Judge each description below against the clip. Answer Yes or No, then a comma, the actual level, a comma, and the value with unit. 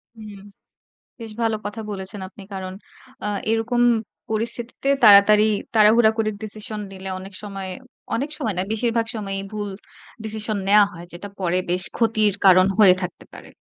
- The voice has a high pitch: Yes, high, 210 Hz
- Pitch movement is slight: Yes, narrow, 2.3 semitones